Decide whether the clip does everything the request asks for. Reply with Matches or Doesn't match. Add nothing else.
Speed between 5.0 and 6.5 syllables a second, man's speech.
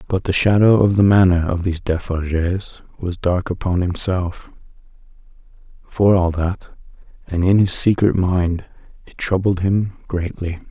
Doesn't match